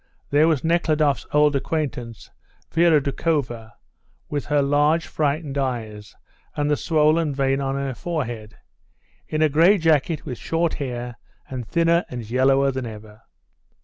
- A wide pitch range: No, average, 3.9 semitones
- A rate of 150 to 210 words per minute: No, average, 140 wpm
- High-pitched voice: No, medium, 140 Hz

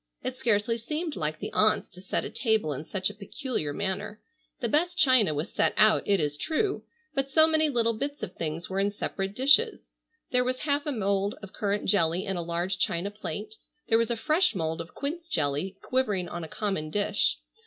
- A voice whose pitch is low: No, high, 210 Hz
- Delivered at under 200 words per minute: No, fast, 205 wpm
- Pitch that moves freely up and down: Yes, wide, 6.2 semitones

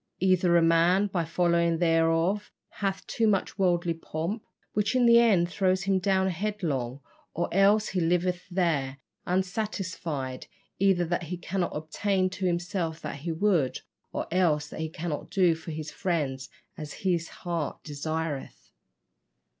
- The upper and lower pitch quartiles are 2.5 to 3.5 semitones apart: Yes, average, 2.8 semitones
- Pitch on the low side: No, medium, 175 Hz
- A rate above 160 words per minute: No, average, 145 wpm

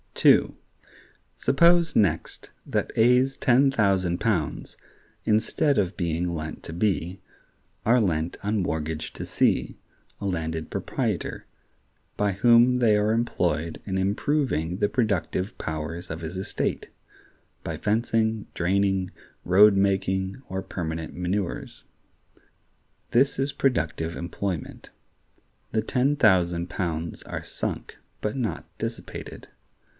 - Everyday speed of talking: No, slow, 115 wpm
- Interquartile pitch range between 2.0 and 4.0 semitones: No, average, 4.7 semitones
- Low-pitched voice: Yes, very low, 95 Hz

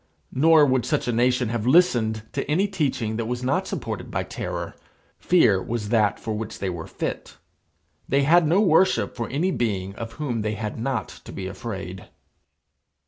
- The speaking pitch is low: Yes, low, 120 Hz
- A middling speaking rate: Yes, average, 180 wpm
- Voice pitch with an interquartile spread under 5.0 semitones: No, wide, 5.4 semitones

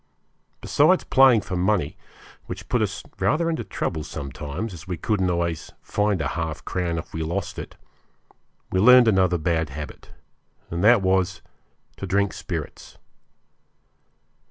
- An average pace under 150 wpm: Yes, average, 140 wpm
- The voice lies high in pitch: No, very low, 90 Hz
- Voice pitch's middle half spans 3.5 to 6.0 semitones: Yes, average, 4.1 semitones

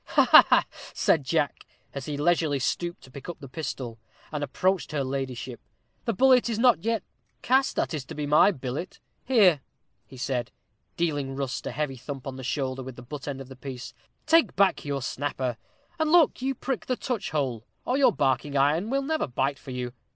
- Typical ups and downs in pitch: No, wide, 6.8 semitones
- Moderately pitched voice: Yes, medium, 145 Hz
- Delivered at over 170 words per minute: Yes, average, 195 wpm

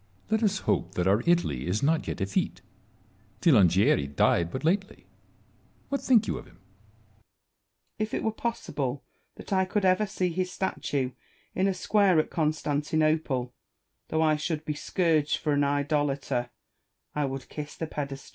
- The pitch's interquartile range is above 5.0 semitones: Yes, wide, 5.6 semitones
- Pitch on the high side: No, medium, 150 Hz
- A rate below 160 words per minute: No, average, 165 wpm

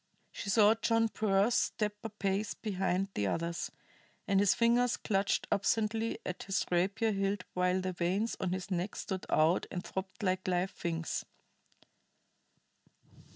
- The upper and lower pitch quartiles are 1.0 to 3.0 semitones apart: Yes, narrow, 2.6 semitones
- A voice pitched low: No, high, 195 Hz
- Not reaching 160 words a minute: Yes, average, 145 wpm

